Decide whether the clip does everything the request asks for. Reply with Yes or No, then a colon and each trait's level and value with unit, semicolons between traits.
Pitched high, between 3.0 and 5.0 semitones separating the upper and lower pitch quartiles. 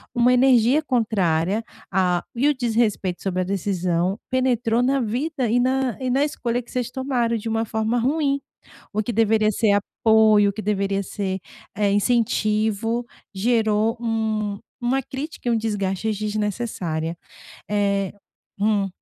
Yes: high, 220 Hz; average, 3.3 semitones